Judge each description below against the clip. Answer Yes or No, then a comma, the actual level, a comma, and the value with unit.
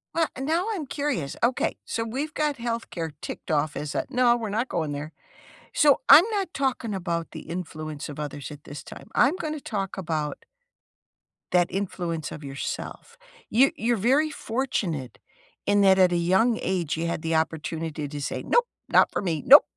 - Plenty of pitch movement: Yes, wide, 8.6 semitones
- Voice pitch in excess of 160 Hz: Yes, high, 190 Hz